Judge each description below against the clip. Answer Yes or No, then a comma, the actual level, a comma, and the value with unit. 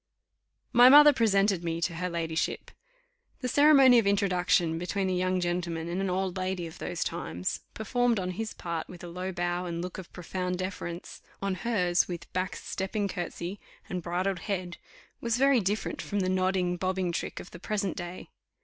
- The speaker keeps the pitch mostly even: Yes, narrow, 2.3 semitones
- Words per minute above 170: Yes, average, 180 wpm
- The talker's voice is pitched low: No, medium, 185 Hz